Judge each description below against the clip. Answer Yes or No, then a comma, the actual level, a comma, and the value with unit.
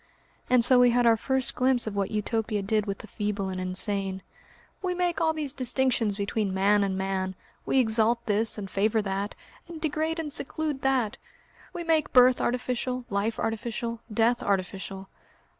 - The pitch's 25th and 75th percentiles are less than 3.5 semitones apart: No, average, 4.2 semitones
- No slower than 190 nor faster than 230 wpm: No, average, 170 wpm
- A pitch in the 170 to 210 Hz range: No, high, 225 Hz